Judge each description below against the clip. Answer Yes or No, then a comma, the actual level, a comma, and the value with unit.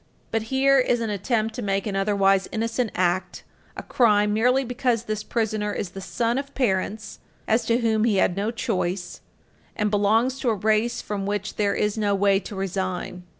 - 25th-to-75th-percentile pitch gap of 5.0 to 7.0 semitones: No, average, 2.8 semitones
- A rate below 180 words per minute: No, average, 190 wpm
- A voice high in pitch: Yes, high, 215 Hz